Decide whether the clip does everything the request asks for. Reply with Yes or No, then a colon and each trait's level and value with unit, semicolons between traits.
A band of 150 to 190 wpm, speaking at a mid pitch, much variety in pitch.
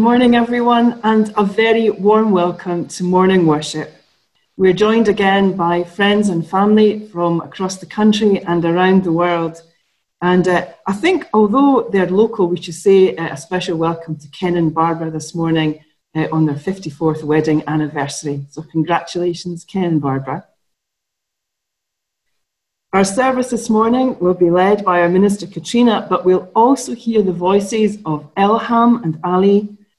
No: average, 155 wpm; medium, 180 Hz; average, 4.3 semitones